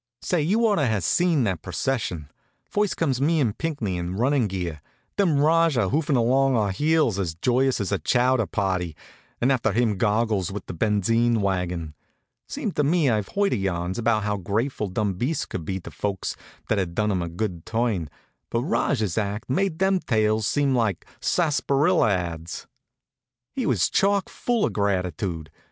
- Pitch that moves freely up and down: Yes, wide, 6.9 semitones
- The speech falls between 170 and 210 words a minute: Yes, average, 175 wpm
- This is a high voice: No, low, 110 Hz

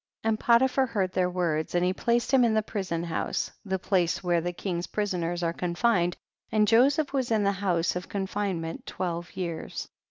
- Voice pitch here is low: No, medium, 185 Hz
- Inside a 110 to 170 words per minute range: No, average, 195 wpm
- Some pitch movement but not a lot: Yes, average, 3.9 semitones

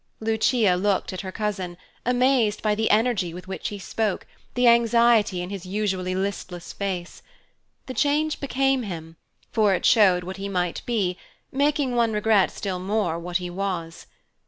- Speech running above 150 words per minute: Yes, average, 160 wpm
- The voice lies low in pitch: No, high, 205 Hz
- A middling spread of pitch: Yes, average, 4.2 semitones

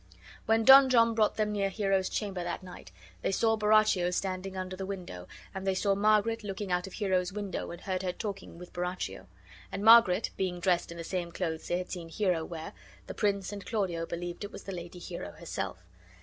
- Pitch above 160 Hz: Yes, high, 190 Hz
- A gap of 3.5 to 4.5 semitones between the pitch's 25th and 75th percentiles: No, average, 2.8 semitones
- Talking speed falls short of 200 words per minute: No, fast, 205 wpm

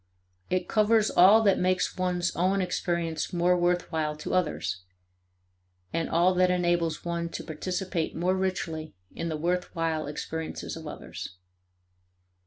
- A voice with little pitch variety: Yes, narrow, 2.1 semitones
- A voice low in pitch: No, medium, 175 Hz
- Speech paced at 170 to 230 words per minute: No, slow, 135 wpm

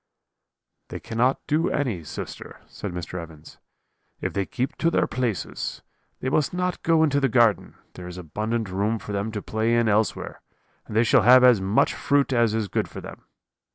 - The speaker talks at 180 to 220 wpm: Yes, average, 190 wpm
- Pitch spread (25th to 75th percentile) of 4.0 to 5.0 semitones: Yes, average, 4.3 semitones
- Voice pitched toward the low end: Yes, low, 115 Hz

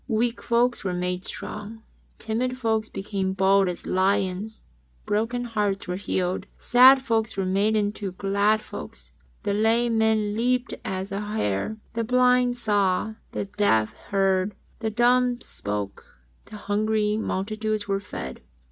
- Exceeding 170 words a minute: No, average, 140 wpm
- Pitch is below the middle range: No, high, 210 Hz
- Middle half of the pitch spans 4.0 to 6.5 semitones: No, average, 2.7 semitones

